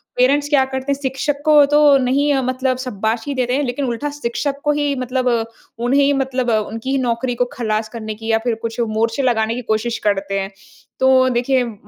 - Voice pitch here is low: No, very high, 250 Hz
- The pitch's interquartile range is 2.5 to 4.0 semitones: Yes, average, 3.3 semitones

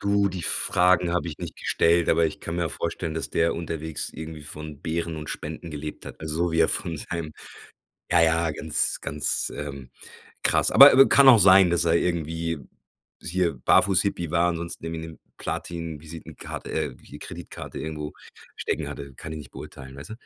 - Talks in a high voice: No, very low, 80 Hz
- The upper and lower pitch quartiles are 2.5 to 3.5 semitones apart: No, narrow, 2.0 semitones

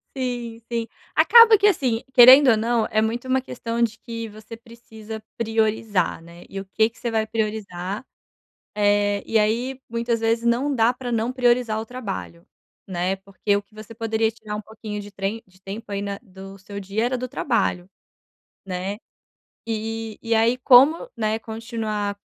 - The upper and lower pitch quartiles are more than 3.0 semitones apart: No, narrow, 2.5 semitones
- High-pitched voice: Yes, high, 225 Hz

